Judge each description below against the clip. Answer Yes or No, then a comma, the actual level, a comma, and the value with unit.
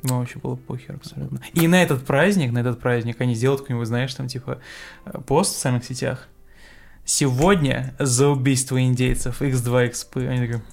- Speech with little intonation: Yes, narrow, 2.0 semitones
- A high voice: No, low, 130 Hz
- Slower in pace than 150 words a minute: No, fast, 160 wpm